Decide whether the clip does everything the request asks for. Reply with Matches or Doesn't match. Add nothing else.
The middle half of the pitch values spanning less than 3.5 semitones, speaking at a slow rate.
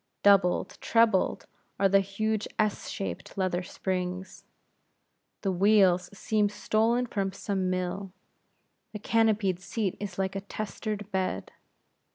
Matches